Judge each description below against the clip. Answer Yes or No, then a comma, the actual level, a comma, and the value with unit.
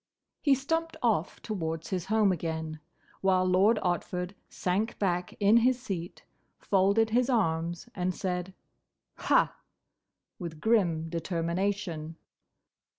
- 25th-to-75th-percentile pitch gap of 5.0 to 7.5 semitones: No, average, 4.3 semitones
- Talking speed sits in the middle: No, slow, 110 wpm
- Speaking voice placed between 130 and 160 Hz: No, medium, 185 Hz